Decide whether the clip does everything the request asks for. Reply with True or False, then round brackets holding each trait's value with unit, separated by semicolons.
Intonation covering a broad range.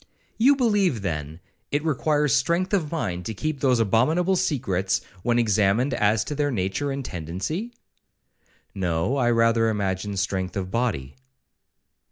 True (7.6 semitones)